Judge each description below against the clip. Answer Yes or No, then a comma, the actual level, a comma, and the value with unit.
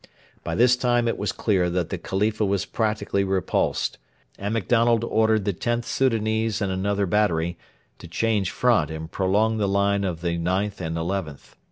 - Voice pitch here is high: No, low, 100 Hz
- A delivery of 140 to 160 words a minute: No, average, 170 wpm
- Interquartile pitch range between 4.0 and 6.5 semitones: No, average, 3.2 semitones